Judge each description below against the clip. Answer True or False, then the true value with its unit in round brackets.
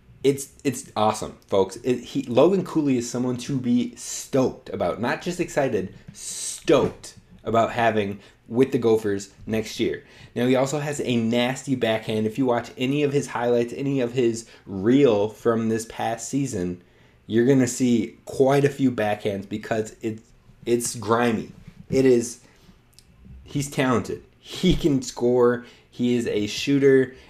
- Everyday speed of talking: True (150 wpm)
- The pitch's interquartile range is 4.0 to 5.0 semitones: False (3.5 semitones)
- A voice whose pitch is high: False (120 Hz)